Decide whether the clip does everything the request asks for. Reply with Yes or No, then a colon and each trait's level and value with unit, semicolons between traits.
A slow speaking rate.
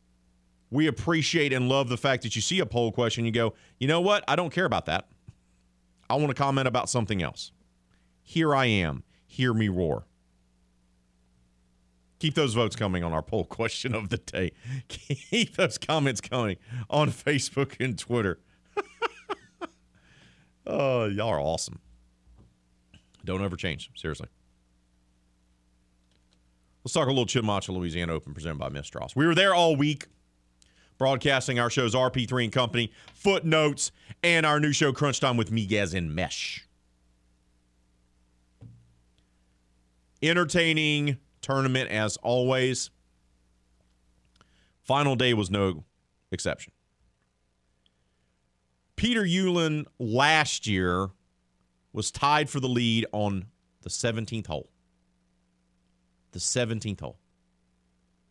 Yes: slow, 120 wpm